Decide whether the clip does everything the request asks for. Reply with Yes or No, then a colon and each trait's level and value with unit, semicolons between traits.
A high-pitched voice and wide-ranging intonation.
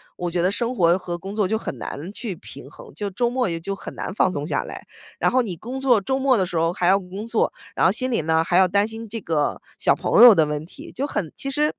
Yes: high, 200 Hz; wide, 5.7 semitones